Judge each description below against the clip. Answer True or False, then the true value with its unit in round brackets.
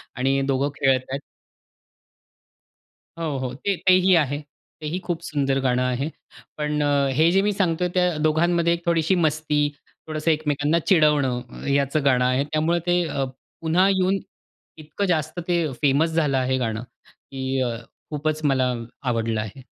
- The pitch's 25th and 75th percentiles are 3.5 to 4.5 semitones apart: True (3.9 semitones)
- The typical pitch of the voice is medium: True (150 Hz)